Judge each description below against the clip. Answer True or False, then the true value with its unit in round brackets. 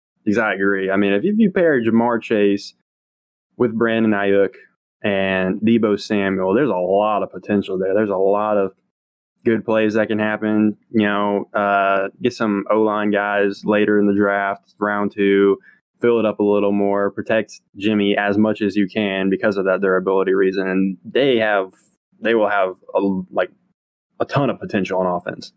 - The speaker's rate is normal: True (180 wpm)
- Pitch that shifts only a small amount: True (1.7 semitones)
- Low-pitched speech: True (100 Hz)